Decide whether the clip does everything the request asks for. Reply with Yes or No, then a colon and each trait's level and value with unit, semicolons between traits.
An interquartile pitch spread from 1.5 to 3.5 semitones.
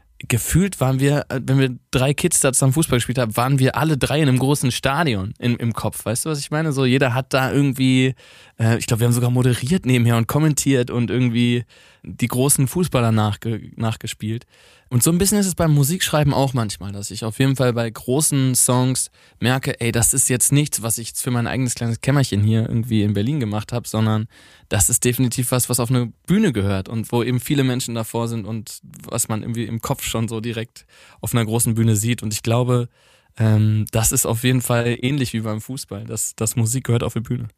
Yes: average, 2.9 semitones